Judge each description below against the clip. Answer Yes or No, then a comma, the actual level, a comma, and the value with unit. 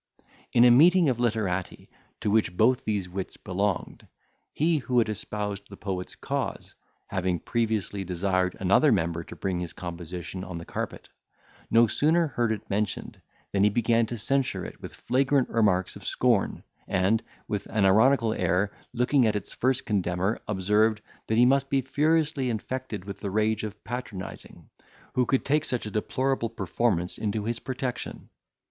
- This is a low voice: Yes, low, 110 Hz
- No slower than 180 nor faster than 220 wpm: No, average, 165 wpm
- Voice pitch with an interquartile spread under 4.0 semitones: No, average, 4.4 semitones